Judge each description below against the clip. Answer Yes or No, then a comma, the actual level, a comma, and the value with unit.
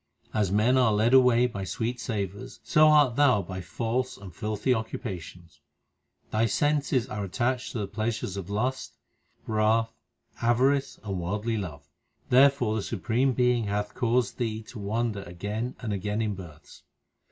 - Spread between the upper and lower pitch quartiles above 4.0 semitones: No, average, 3.6 semitones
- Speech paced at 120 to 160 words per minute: Yes, average, 150 wpm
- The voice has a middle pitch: No, low, 110 Hz